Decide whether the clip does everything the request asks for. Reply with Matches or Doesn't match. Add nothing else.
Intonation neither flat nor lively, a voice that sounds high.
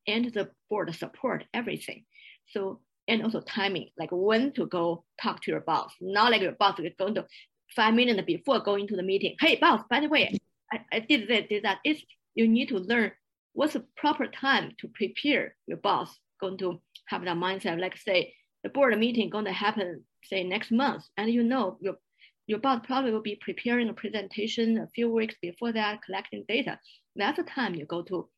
Matches